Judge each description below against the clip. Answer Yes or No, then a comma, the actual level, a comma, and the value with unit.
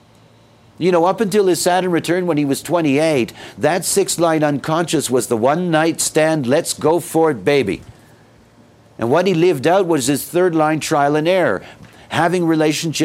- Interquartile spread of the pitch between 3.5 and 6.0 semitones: Yes, average, 3.9 semitones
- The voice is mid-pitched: Yes, medium, 155 Hz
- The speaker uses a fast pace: No, average, 165 wpm